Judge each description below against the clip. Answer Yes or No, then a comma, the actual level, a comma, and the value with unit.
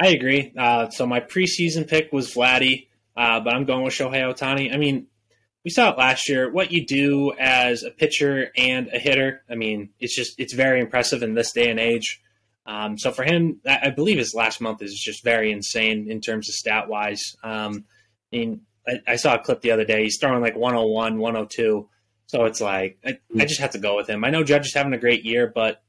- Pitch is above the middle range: No, low, 120 Hz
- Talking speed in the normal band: No, fast, 230 wpm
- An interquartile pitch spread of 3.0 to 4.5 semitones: Yes, average, 3.4 semitones